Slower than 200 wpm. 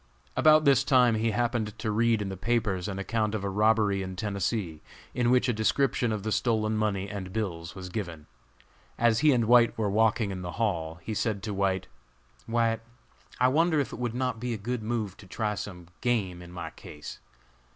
No: fast, 205 wpm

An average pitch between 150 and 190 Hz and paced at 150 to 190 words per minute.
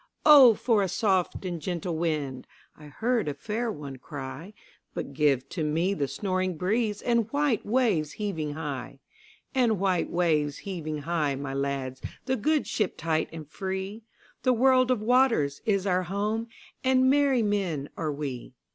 No: medium, 185 Hz; average, 140 wpm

